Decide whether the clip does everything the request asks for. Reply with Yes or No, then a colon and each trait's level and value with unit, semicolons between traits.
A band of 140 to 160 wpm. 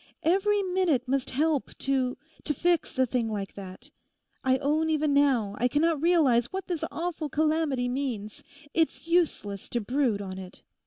Yes: average, 155 wpm